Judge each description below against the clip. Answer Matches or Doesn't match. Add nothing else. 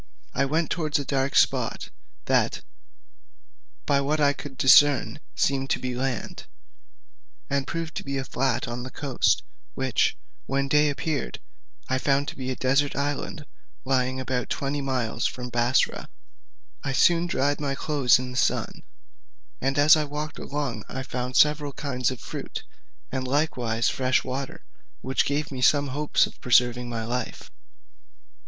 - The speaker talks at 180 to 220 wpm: Doesn't match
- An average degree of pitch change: Doesn't match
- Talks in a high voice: Doesn't match